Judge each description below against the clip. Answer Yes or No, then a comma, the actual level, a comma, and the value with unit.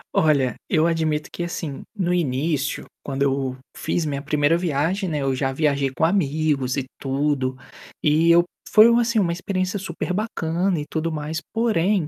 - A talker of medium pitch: Yes, medium, 155 Hz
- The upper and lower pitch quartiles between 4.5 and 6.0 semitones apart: No, average, 3.8 semitones